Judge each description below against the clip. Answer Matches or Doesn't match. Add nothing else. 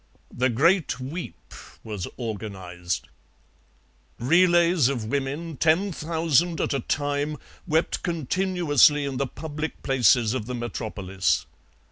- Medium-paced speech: Doesn't match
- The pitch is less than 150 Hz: Matches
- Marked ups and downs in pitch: Matches